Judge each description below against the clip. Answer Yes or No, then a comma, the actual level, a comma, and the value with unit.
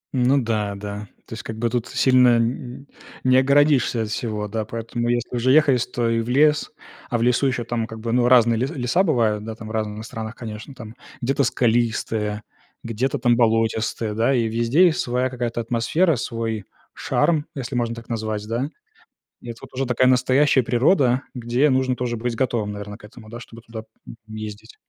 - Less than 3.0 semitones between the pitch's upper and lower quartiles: Yes, narrow, 2.4 semitones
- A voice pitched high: No, low, 120 Hz